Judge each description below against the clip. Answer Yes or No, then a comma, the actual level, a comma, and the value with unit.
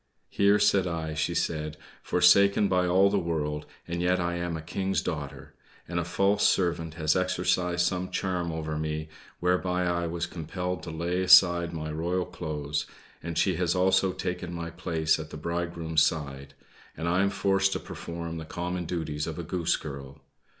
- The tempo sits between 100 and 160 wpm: No, average, 180 wpm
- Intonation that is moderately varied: No, narrow, 2.3 semitones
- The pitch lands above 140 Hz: No, very low, 85 Hz